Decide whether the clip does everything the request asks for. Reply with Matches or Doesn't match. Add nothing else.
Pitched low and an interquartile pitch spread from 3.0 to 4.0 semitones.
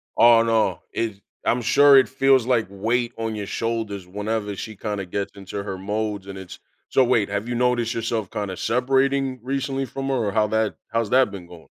Matches